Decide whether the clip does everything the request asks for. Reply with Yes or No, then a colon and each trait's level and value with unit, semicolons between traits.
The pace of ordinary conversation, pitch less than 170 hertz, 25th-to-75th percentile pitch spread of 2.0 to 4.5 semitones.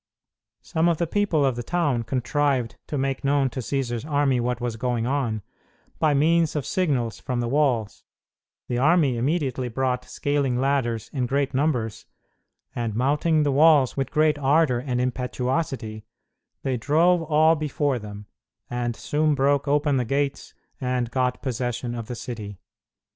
Yes: average, 155 wpm; low, 135 Hz; average, 3.2 semitones